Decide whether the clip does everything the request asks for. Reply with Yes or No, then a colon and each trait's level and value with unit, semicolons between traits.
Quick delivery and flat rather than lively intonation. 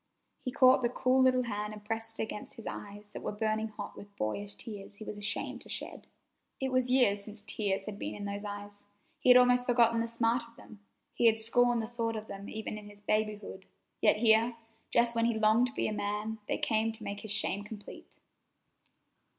Yes: fast, 215 wpm; narrow, 2.2 semitones